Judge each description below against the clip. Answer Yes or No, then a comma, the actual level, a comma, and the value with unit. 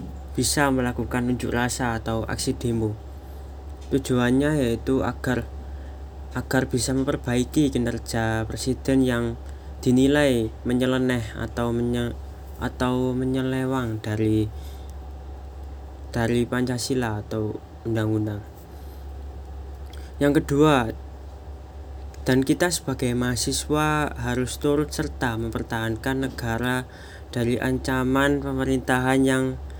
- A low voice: Yes, low, 120 Hz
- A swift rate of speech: No, slow, 85 wpm